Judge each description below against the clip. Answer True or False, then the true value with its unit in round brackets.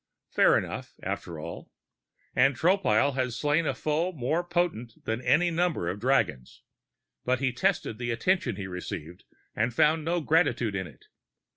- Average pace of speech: True (155 wpm)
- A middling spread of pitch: False (7.1 semitones)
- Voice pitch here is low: True (130 Hz)